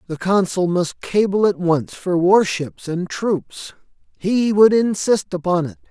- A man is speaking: Yes, male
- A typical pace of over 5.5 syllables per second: No, 3.9 syllables/s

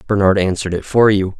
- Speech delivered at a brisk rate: Yes, fast, 215 wpm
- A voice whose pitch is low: Yes, very low, 95 Hz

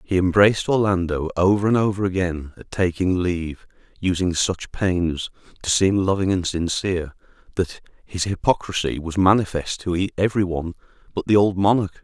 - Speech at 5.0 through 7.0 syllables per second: Yes, 5.3 syllables/s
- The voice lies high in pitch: No, very low, 95 Hz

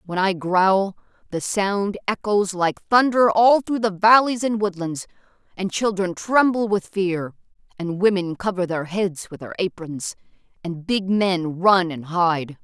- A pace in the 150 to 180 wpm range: Yes, average, 155 wpm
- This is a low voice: No, high, 190 Hz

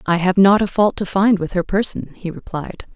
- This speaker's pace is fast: Yes, fast, 245 wpm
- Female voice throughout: Yes, female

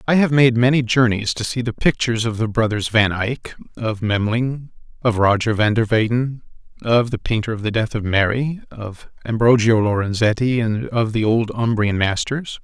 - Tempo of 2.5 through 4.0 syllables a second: No, 4.9 syllables/s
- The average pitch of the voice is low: Yes, low, 115 Hz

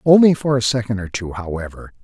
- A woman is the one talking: No, male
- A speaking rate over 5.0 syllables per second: Yes, 5.9 syllables/s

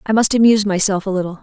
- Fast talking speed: Yes, fast, 255 wpm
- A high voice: Yes, high, 200 Hz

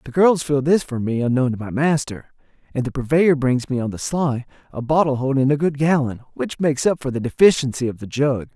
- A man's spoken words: Yes, male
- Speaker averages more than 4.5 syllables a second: Yes, 5.7 syllables/s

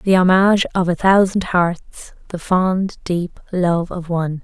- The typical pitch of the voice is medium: Yes, medium, 180 Hz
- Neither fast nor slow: Yes, average, 160 wpm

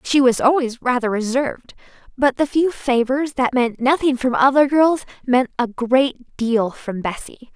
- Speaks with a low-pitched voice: No, very high, 255 Hz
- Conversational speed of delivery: Yes, average, 165 wpm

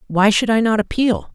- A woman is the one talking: No, male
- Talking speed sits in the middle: No, fast, 225 wpm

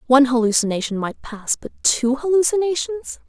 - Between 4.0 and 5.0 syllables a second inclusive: No, 5.3 syllables/s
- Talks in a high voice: Yes, very high, 275 Hz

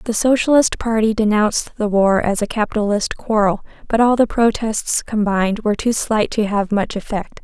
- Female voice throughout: Yes, female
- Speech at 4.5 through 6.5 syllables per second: Yes, 5.0 syllables/s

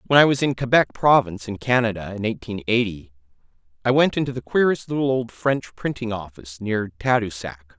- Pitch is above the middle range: No, low, 110 Hz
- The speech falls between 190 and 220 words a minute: No, average, 175 wpm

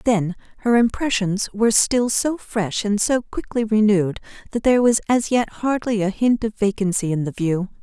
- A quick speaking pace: No, average, 185 wpm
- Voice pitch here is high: Yes, high, 215 Hz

